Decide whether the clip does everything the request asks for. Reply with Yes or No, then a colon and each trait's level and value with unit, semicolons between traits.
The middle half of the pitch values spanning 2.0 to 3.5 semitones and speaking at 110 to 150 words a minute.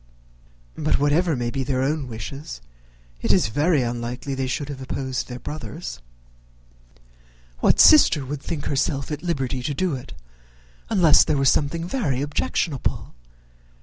Yes: average, 3.1 semitones; average, 145 wpm